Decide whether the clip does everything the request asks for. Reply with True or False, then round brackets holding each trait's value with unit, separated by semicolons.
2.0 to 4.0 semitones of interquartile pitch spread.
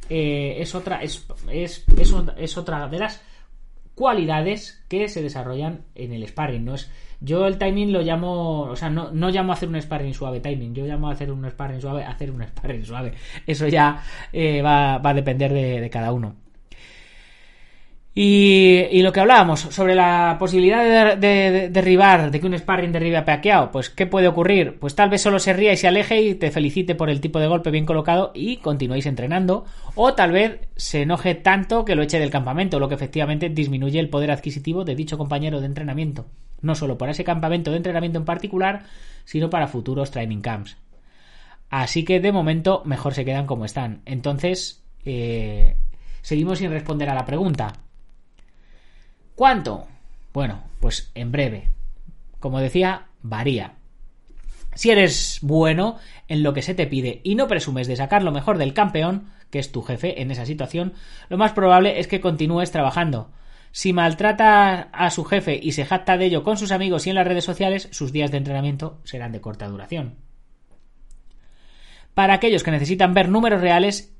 False (5.1 semitones)